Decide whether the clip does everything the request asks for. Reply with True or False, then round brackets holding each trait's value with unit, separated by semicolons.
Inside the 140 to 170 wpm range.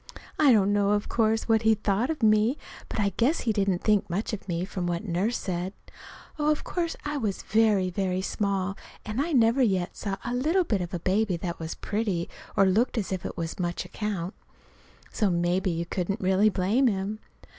False (200 wpm)